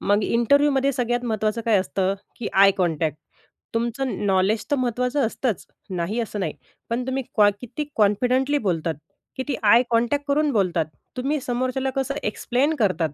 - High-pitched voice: Yes, high, 235 Hz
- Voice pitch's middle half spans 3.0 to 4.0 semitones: No, average, 4.6 semitones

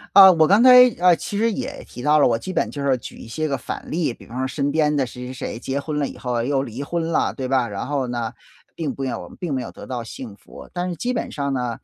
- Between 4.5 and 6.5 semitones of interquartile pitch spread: Yes, average, 5.1 semitones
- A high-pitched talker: No, medium, 140 Hz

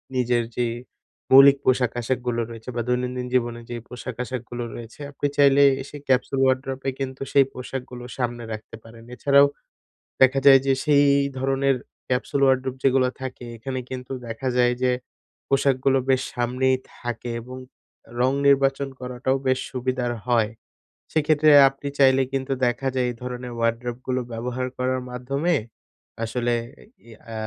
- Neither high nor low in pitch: No, low, 130 Hz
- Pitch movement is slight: Yes, narrow, 1.7 semitones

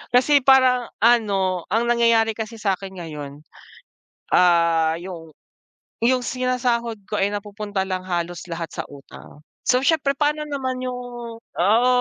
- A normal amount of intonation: No, wide, 5.7 semitones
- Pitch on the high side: Yes, high, 225 Hz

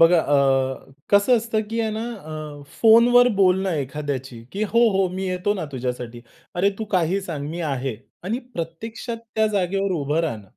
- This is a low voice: No, medium, 185 Hz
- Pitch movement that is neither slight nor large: No, wide, 6.9 semitones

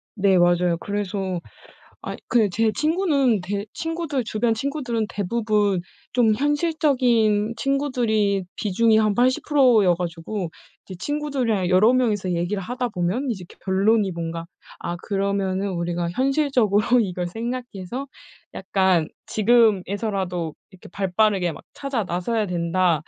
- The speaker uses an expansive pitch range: No, average, 4.9 semitones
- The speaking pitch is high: Yes, high, 210 Hz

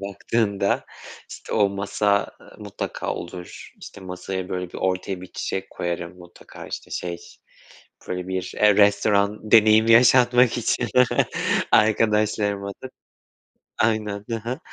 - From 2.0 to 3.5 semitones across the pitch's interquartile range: Yes, average, 2.7 semitones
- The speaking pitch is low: Yes, low, 100 Hz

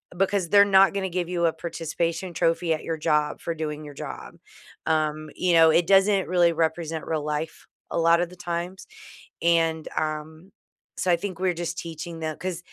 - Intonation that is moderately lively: No, narrow, 2.0 semitones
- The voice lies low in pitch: No, medium, 170 Hz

